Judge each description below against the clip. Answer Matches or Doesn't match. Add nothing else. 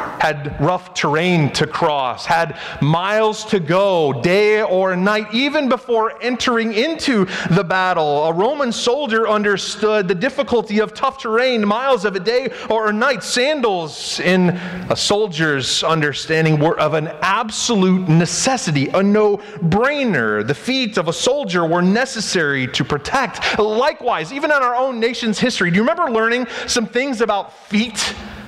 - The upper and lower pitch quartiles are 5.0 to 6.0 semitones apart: Matches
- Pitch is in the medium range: Doesn't match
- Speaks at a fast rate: Doesn't match